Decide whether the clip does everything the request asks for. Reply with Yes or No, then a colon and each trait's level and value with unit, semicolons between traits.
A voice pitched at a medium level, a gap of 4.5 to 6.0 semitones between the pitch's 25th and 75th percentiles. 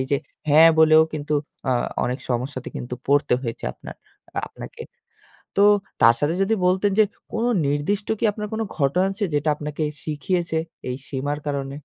Yes: medium, 150 Hz; average, 4.9 semitones